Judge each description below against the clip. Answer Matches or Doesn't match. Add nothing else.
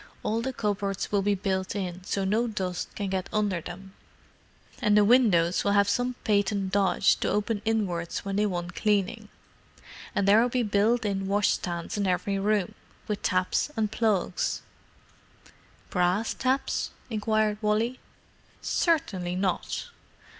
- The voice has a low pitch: Doesn't match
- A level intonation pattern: Matches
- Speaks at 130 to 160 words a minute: Matches